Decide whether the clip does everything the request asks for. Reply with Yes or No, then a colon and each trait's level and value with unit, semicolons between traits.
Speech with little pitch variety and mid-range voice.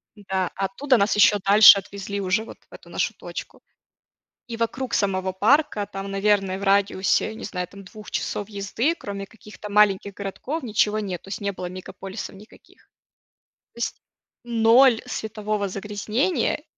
No: narrow, 2.0 semitones; high, 205 Hz